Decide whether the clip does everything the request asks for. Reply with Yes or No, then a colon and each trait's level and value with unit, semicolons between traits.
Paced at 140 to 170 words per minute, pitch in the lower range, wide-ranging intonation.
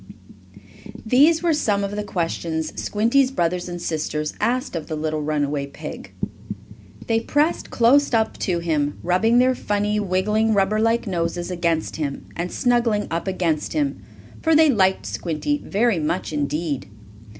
No: average, 150 wpm; high, 190 Hz; wide, 6.1 semitones